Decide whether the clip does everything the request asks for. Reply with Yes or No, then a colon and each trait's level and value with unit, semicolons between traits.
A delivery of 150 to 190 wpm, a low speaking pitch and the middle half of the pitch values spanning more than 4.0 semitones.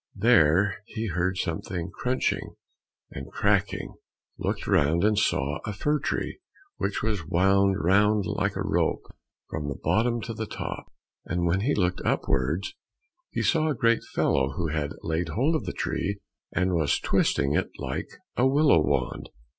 Yes: average, 160 wpm; very low, 95 Hz; wide, 5.5 semitones